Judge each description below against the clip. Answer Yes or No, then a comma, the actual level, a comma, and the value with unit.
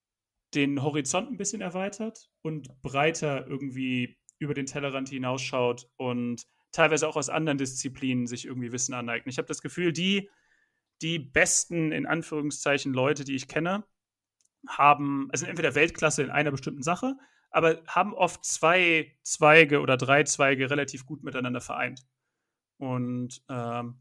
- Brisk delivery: No, average, 145 wpm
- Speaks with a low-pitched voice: No, medium, 145 Hz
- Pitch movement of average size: Yes, average, 3.6 semitones